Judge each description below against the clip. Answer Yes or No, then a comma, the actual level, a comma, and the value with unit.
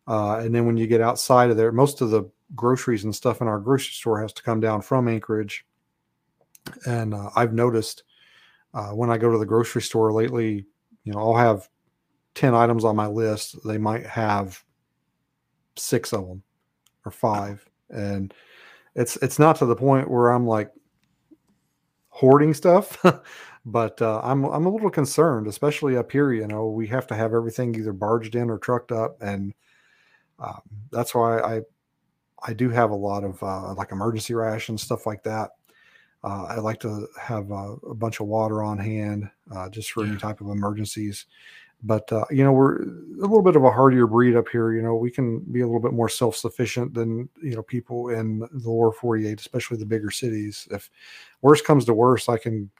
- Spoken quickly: No, average, 195 wpm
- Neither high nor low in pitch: No, low, 115 Hz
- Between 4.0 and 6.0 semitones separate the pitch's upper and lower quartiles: No, narrow, 2.4 semitones